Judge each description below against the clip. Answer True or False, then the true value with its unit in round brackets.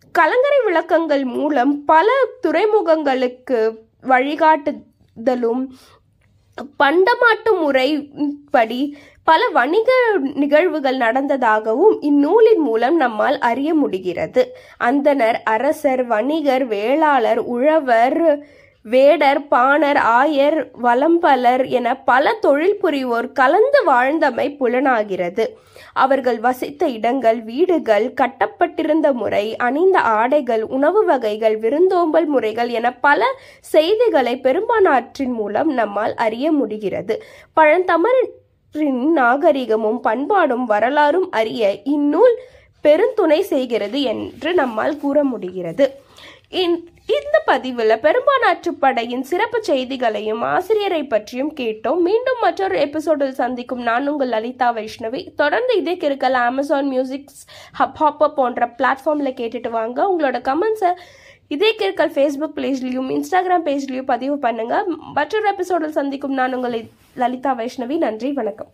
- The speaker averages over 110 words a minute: False (95 wpm)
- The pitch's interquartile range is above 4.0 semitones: True (5.1 semitones)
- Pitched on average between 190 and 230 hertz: False (285 Hz)